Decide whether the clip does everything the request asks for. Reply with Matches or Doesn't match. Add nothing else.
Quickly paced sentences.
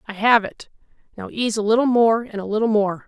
Matches